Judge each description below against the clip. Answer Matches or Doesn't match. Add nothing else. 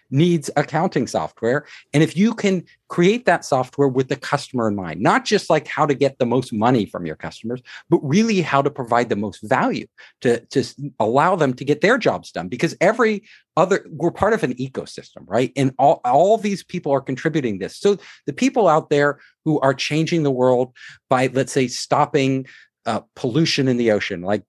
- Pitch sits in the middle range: Matches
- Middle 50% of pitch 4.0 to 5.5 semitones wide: Matches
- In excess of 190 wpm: Matches